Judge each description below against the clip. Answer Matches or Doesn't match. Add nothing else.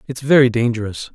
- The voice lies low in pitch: Matches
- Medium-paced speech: Matches